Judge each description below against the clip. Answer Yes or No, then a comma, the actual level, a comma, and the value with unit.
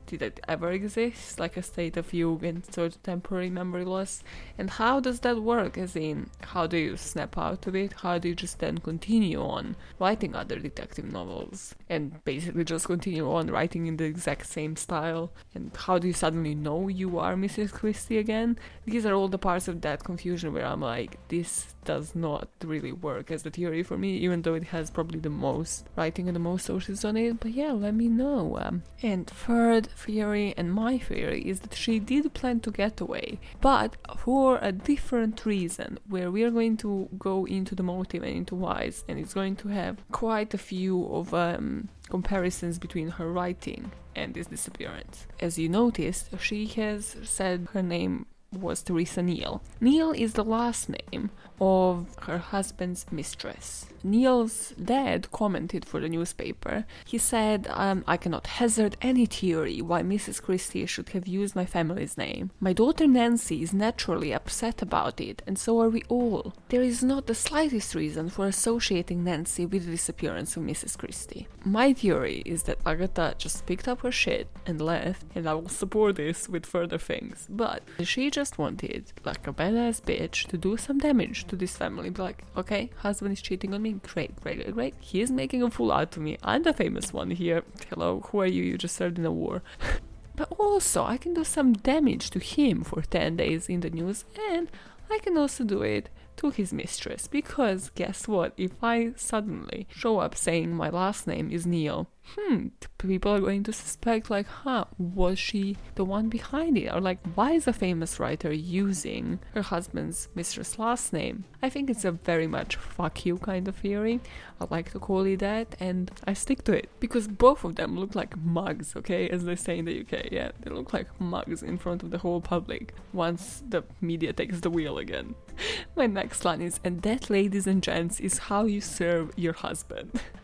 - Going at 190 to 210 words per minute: Yes, average, 195 wpm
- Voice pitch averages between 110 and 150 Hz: No, high, 190 Hz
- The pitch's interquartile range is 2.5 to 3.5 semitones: No, average, 4.8 semitones